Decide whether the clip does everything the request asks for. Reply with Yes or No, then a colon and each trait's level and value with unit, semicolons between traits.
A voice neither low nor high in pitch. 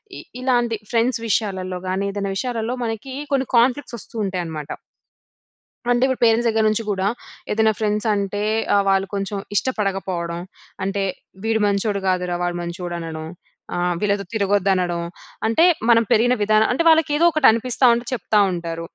No: high, 205 Hz